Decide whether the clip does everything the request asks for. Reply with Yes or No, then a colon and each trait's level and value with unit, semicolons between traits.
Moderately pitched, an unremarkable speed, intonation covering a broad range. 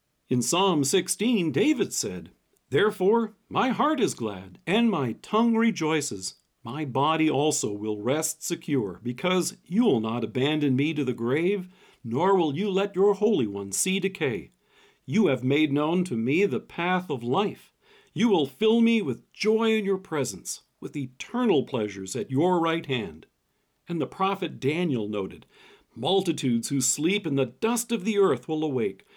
Yes: medium, 165 Hz; average, 165 wpm; wide, 7.1 semitones